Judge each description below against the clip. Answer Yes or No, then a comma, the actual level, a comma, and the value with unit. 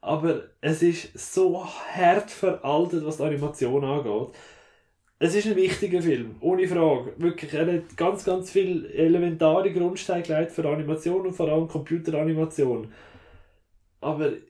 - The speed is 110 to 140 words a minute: Yes, average, 130 wpm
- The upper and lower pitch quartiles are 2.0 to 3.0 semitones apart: No, average, 3.4 semitones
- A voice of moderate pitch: Yes, medium, 165 Hz